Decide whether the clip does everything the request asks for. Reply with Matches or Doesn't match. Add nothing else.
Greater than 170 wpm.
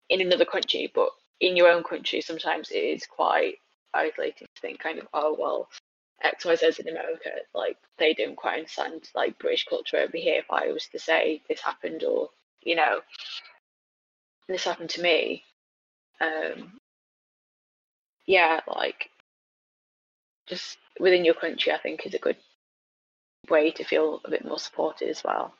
Doesn't match